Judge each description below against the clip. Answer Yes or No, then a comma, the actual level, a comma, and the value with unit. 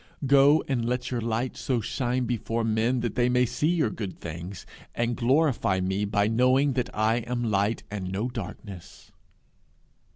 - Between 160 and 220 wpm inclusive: Yes, average, 165 wpm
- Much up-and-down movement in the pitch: No, average, 3.2 semitones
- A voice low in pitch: Yes, low, 120 Hz